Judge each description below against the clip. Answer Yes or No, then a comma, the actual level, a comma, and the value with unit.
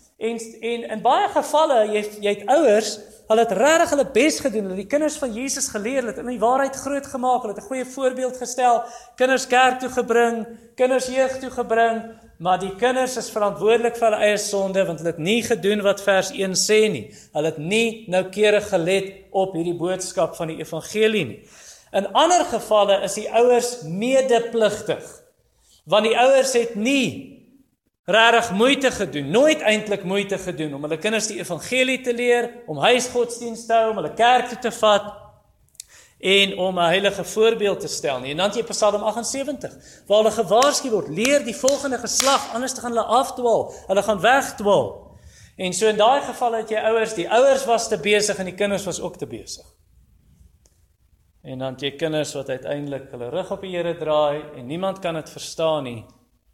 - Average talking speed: Yes, average, 185 wpm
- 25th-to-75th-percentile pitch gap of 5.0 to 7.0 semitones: No, average, 4.6 semitones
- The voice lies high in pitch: Yes, high, 220 Hz